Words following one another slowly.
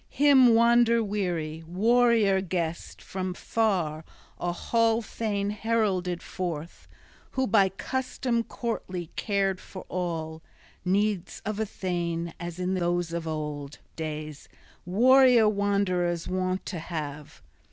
Yes: slow, 110 wpm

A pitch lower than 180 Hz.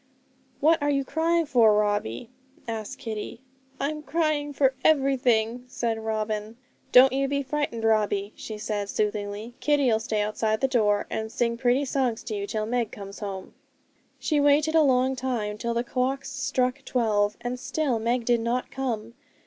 No: high, 240 Hz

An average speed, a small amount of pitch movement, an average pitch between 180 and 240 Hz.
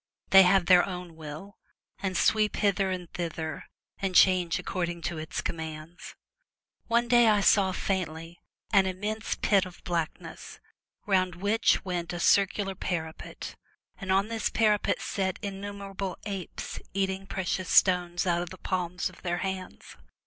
Yes: average, 150 wpm; narrow, 2.2 semitones; medium, 185 Hz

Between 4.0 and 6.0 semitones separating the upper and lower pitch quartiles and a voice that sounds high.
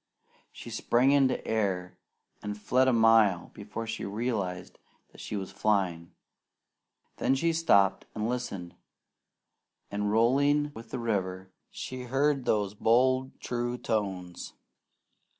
No: average, 4.3 semitones; low, 110 Hz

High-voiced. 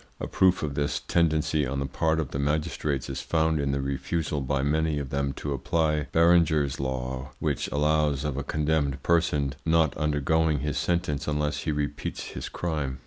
No: very low, 75 Hz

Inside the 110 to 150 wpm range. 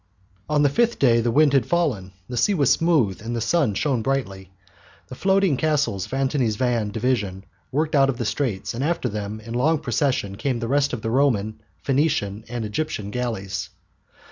No: average, 190 wpm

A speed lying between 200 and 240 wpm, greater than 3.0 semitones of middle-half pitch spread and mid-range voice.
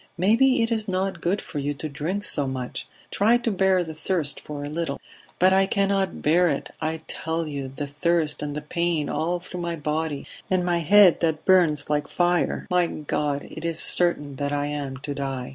Yes: fast, 205 wpm; average, 3.8 semitones; medium, 160 Hz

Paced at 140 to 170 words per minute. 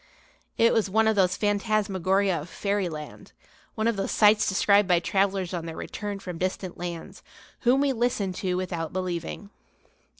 Yes: average, 160 wpm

